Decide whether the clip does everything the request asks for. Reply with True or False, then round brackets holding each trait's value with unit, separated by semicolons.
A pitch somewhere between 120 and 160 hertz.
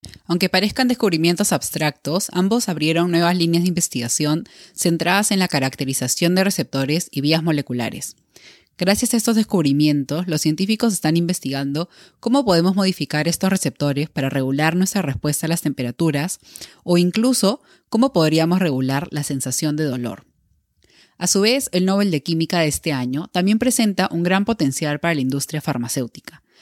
False (170 Hz)